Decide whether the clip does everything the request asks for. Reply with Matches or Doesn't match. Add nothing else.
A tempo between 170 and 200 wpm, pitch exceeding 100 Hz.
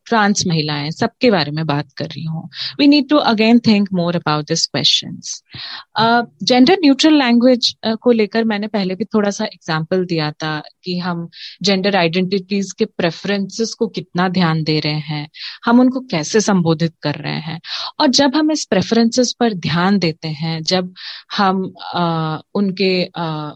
Doesn't match